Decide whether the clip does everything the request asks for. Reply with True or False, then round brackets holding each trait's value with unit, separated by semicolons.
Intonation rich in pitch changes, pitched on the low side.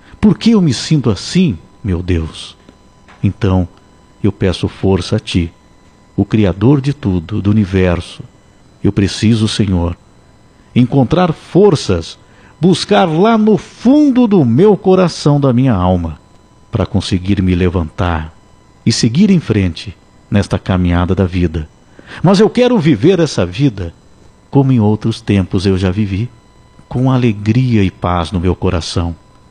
True (7.1 semitones; 100 Hz)